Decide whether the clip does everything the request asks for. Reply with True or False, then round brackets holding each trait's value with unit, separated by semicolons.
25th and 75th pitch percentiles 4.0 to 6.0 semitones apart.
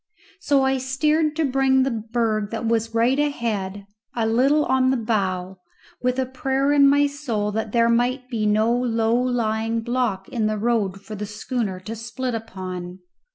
False (3.4 semitones)